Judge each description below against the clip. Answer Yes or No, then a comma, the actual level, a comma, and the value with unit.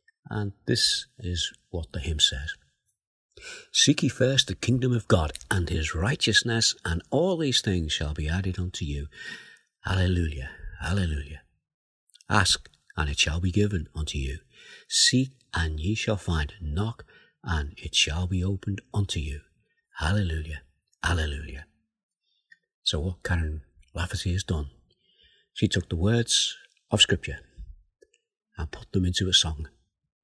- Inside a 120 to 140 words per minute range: Yes, slow, 135 wpm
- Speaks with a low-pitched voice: Yes, very low, 95 Hz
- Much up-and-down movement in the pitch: Yes, wide, 6.3 semitones